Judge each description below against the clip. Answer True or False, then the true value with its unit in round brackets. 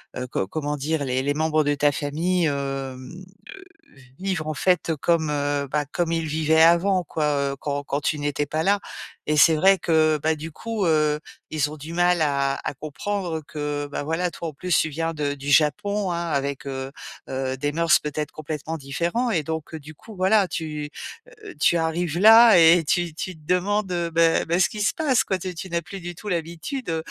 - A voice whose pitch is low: False (160 Hz)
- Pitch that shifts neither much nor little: True (3.2 semitones)